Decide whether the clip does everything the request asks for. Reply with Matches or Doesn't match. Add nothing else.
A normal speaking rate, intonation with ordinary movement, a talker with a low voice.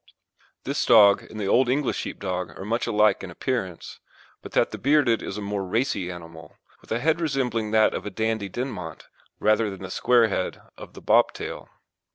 Matches